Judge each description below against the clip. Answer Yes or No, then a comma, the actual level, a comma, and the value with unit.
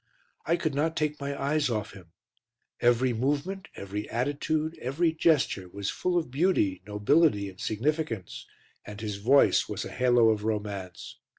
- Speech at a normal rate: Yes, average, 155 wpm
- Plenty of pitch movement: Yes, wide, 6.7 semitones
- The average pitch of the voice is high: No, low, 125 Hz